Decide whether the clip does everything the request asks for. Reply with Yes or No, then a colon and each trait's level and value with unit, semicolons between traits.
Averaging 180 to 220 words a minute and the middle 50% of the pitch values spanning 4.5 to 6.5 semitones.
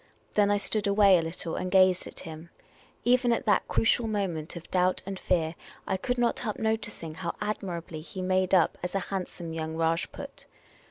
No: average, 185 wpm; average, 3.7 semitones